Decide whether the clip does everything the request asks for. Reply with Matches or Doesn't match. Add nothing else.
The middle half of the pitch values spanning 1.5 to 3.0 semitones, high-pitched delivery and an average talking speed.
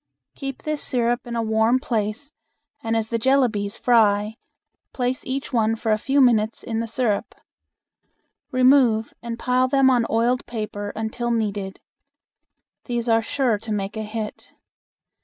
Matches